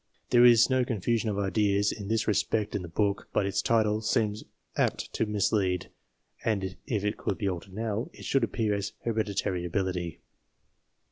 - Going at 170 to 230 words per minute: Yes, average, 175 wpm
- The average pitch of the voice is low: Yes, low, 105 Hz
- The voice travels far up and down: No, narrow, 2.4 semitones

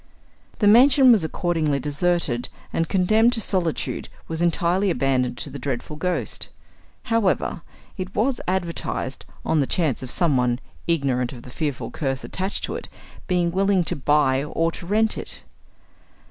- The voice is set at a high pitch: No, medium, 165 Hz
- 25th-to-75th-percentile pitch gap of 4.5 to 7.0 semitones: Yes, wide, 5.5 semitones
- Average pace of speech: Yes, average, 150 wpm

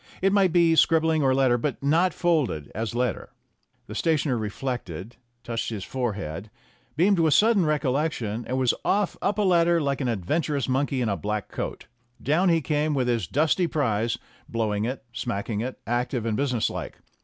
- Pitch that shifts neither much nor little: No, wide, 5.9 semitones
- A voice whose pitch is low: Yes, low, 130 Hz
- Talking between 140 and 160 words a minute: No, average, 175 wpm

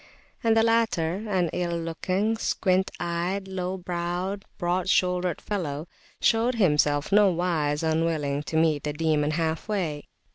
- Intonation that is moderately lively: Yes, average, 3.2 semitones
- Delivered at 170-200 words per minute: No, slow, 135 wpm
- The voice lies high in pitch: No, medium, 175 Hz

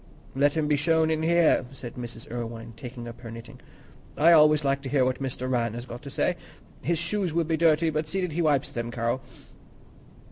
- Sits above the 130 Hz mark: Yes, medium, 140 Hz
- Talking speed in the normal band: No, fast, 215 wpm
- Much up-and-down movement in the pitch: No, average, 4.9 semitones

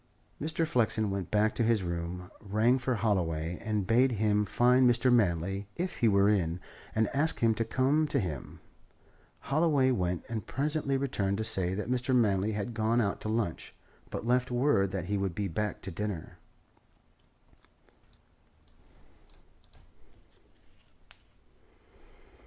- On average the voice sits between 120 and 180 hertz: No, low, 110 Hz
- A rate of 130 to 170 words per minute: Yes, average, 140 wpm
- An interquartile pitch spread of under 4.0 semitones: No, average, 4.3 semitones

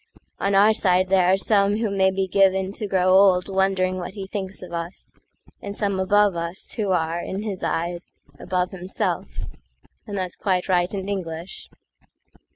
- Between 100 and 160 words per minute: Yes, average, 155 wpm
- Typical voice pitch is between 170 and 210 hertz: Yes, high, 190 Hz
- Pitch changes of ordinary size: No, narrow, 1.6 semitones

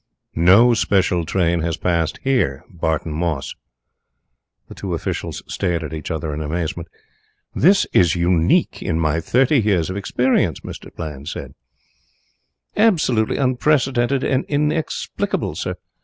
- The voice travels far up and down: Yes, wide, 7.9 semitones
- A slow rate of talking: Yes, slow, 125 wpm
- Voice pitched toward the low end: Yes, very low, 90 Hz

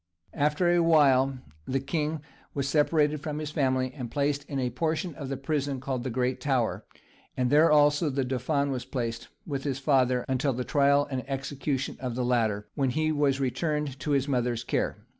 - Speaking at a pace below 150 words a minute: No, average, 190 wpm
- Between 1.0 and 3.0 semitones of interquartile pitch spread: Yes, narrow, 2.6 semitones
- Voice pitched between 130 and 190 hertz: Yes, medium, 140 Hz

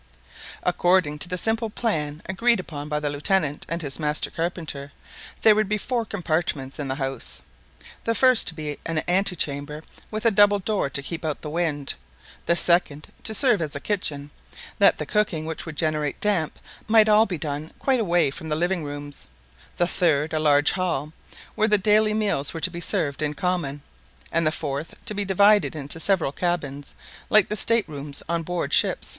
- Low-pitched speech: No, medium, 165 Hz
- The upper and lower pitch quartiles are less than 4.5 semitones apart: No, average, 5.3 semitones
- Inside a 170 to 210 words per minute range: Yes, average, 190 wpm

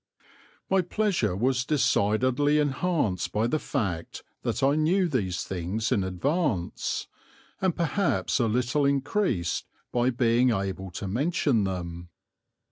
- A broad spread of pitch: Yes, wide, 7.6 semitones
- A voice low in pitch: Yes, low, 125 Hz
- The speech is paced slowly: Yes, slow, 125 wpm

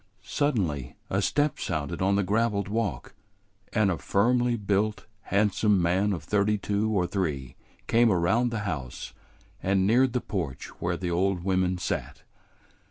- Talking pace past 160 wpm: No, average, 150 wpm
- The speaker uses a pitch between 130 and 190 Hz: No, low, 100 Hz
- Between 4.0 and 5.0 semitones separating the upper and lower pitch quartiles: No, average, 3.6 semitones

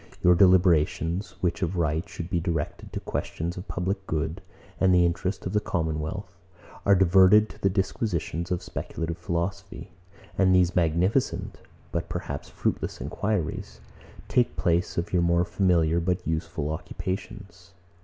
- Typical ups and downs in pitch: No, narrow, 2.2 semitones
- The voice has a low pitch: Yes, very low, 90 Hz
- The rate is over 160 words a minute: No, average, 145 wpm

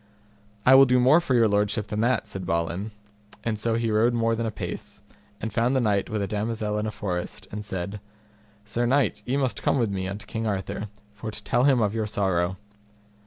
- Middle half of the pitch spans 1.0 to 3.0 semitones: Yes, average, 2.7 semitones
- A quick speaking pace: Yes, fast, 215 wpm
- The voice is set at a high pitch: No, low, 110 Hz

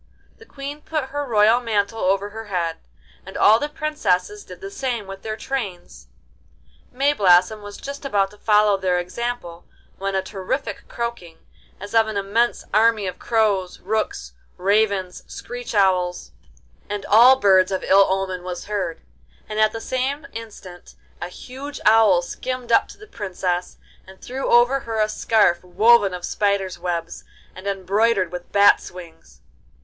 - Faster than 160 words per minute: No, average, 155 wpm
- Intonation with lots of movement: No, average, 4.1 semitones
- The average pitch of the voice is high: Yes, high, 205 Hz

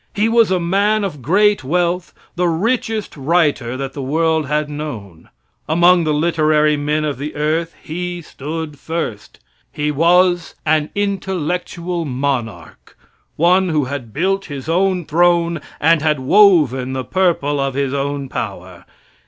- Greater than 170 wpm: No, average, 145 wpm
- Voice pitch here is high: No, medium, 155 Hz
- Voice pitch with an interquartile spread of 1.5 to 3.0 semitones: No, average, 4.0 semitones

